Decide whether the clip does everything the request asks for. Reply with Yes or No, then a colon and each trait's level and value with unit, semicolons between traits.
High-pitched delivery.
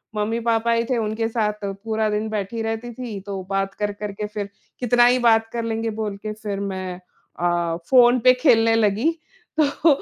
Yes: high, 220 Hz